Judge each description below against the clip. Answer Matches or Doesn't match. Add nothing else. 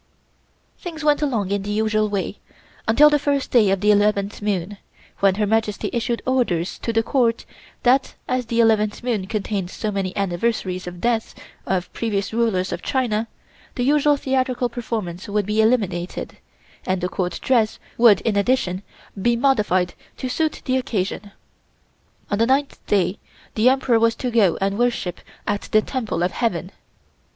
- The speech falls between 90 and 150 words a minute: Doesn't match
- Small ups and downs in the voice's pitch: Doesn't match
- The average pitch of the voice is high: Matches